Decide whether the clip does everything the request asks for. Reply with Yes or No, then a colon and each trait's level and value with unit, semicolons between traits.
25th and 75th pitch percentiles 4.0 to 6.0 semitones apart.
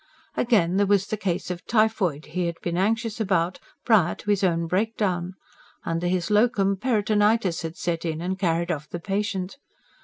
No: average, 3.4 semitones